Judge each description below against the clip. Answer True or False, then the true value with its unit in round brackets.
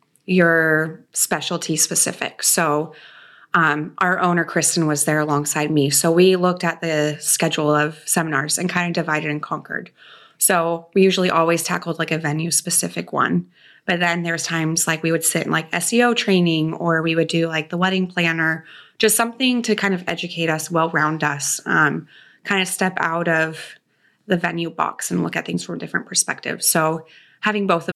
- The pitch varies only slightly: True (2.3 semitones)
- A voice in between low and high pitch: True (165 Hz)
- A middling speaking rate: True (185 wpm)